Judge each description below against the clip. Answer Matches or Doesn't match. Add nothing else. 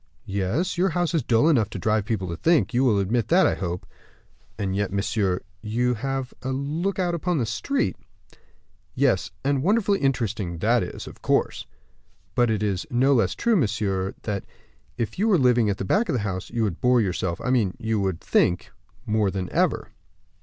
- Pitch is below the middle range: Matches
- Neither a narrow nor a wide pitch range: Doesn't match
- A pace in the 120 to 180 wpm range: Doesn't match